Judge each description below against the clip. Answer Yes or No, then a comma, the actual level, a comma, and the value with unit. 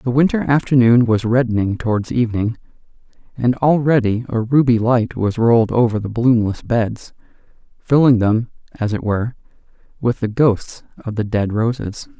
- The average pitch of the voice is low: Yes, low, 115 Hz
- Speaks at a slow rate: No, average, 150 wpm